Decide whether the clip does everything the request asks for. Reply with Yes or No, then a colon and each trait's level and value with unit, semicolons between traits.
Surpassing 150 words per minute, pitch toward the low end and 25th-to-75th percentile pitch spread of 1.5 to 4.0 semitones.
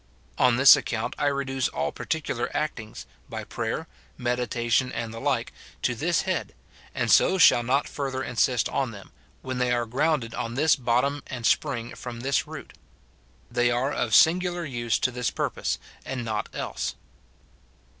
Yes: average, 160 wpm; low, 125 Hz; average, 2.9 semitones